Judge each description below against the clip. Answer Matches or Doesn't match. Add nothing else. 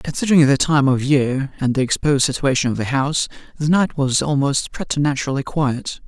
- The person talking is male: Matches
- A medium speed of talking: Matches